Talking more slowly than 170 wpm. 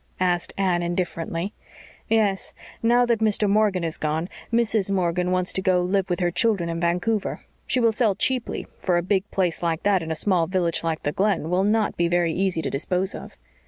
No: fast, 205 wpm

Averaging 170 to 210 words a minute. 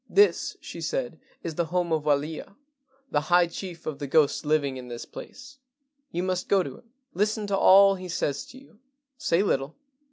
Yes: average, 190 wpm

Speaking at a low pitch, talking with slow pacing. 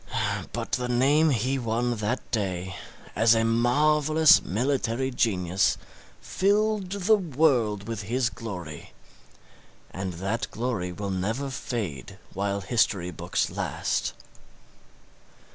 Yes: low, 115 Hz; slow, 110 wpm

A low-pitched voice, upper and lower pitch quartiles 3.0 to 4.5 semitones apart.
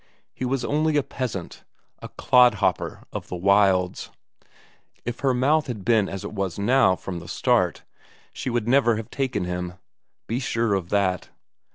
No: low, 110 Hz; average, 5.2 semitones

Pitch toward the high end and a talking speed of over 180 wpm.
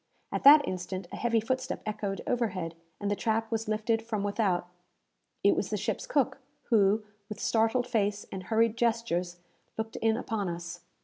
No: high, 220 Hz; average, 170 wpm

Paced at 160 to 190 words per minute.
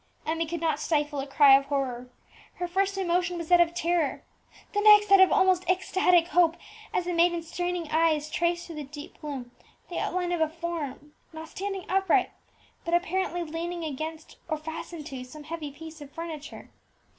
Yes: average, 180 wpm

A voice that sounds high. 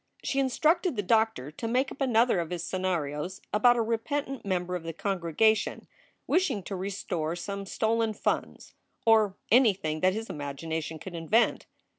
Yes: high, 200 Hz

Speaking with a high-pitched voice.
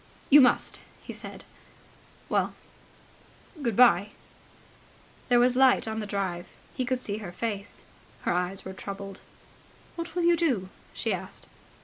Yes: high, 220 Hz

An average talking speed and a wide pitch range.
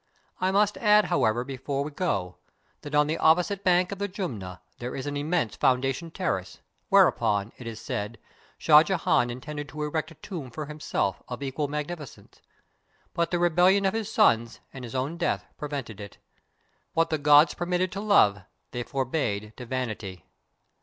Yes: average, 170 wpm; wide, 6.2 semitones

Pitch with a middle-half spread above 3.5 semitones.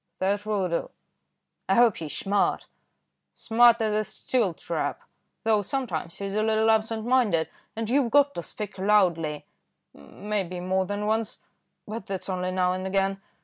No: average, 3.1 semitones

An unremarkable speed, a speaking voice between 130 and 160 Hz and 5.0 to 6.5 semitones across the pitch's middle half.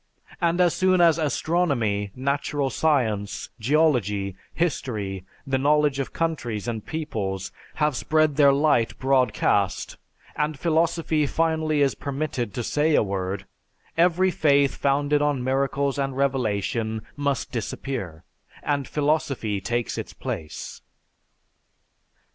No: slow, 115 wpm; medium, 140 Hz; average, 5.3 semitones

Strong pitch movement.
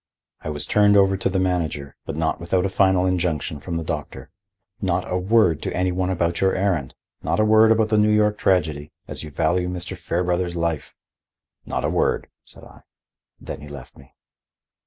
No: average, 3.0 semitones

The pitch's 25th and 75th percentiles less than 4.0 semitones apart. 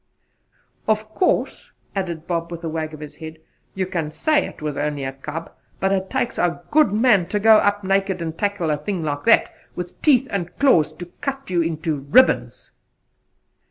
No: average, 4.6 semitones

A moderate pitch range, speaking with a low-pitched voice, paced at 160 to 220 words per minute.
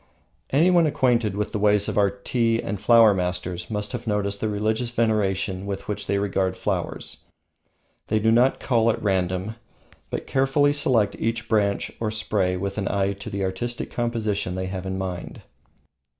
Yes: average, 3.1 semitones; low, 105 Hz; average, 170 wpm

